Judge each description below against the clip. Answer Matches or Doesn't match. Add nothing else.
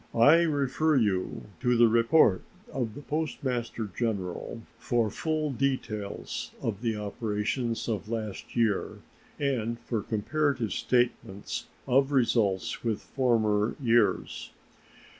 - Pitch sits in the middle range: Doesn't match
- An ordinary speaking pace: Doesn't match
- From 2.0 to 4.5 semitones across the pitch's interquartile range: Matches